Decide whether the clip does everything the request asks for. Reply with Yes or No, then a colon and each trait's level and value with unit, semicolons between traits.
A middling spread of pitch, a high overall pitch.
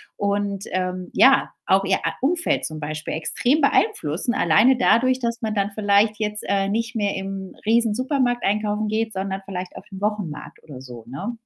Yes: average, 3.5 semitones; high, 205 Hz